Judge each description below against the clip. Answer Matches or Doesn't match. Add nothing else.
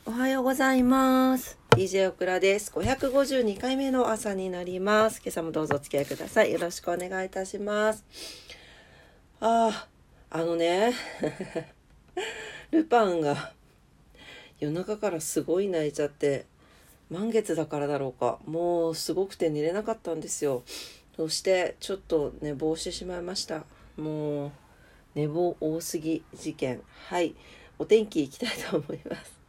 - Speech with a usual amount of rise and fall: Doesn't match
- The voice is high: Doesn't match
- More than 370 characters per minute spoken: Doesn't match